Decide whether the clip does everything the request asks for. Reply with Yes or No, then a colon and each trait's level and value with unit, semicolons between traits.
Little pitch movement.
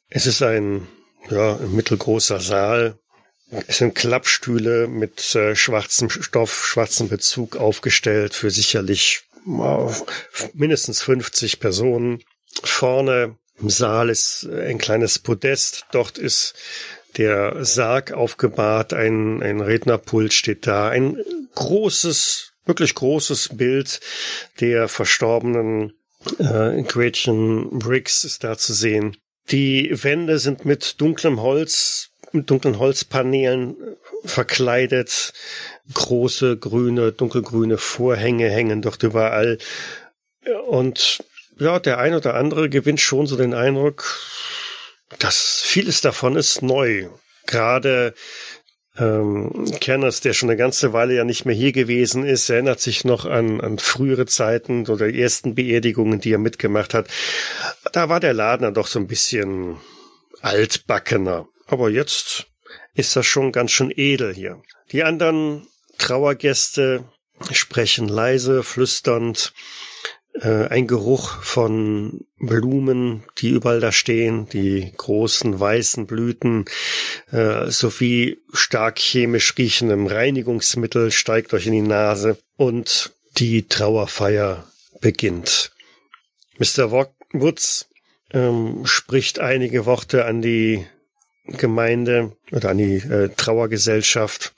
No: average, 3.0 semitones